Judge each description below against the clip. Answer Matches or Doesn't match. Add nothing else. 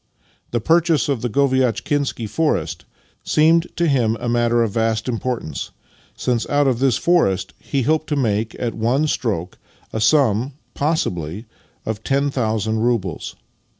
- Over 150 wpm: Doesn't match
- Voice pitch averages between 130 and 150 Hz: Doesn't match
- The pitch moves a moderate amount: Matches